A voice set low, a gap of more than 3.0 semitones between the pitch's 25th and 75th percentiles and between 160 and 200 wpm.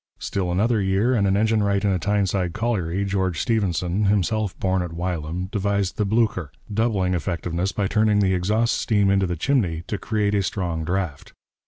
No: low, 100 Hz; average, 2.7 semitones; average, 180 wpm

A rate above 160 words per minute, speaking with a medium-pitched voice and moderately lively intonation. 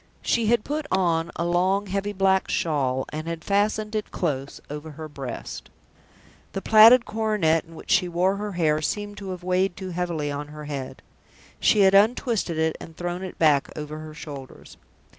Yes: average, 180 wpm; medium, 175 Hz; average, 4.6 semitones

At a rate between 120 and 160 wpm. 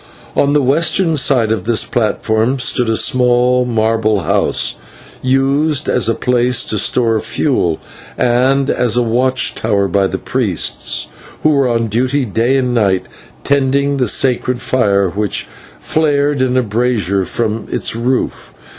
Yes: average, 145 wpm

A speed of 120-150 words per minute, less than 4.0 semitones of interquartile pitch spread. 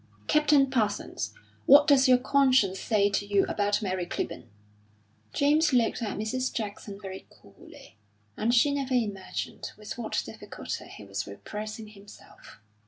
No: average, 140 wpm; average, 4.5 semitones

